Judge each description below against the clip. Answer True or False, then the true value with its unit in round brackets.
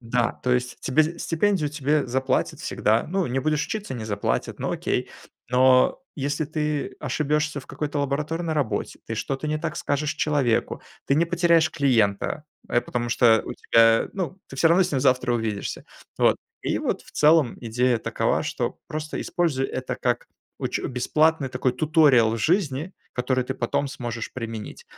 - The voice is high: False (140 Hz)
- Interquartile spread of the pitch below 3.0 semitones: False (3.8 semitones)